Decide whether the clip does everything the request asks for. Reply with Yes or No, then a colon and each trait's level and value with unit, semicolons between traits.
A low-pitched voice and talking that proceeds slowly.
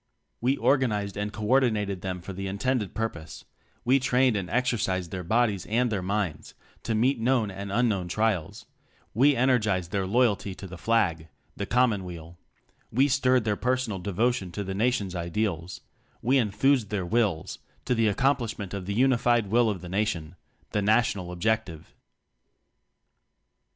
No: low, 105 Hz; average, 165 wpm